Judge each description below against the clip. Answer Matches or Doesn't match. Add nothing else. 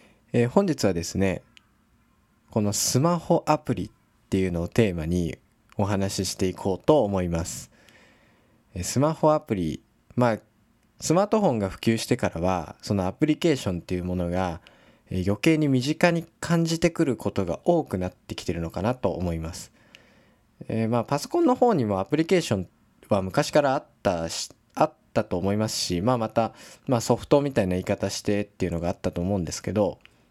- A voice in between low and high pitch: Doesn't match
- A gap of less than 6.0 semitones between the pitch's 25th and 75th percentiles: Matches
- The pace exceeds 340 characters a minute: Matches